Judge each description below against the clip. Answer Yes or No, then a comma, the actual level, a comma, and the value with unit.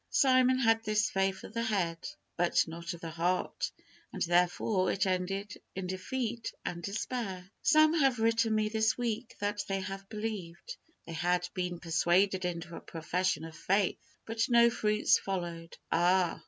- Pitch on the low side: No, high, 195 Hz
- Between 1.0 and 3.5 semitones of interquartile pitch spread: No, average, 4.2 semitones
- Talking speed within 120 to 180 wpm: Yes, average, 160 wpm